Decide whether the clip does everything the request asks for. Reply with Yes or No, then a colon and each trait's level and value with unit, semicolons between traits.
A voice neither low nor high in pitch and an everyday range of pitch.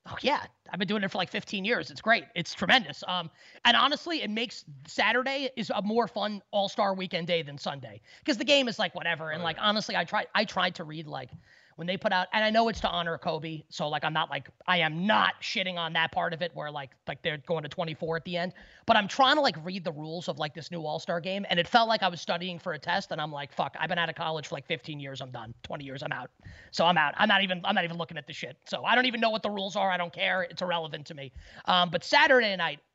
Yes: medium, 175 Hz; average, 4.5 semitones